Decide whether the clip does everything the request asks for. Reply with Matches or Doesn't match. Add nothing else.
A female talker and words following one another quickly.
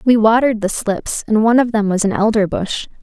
Matches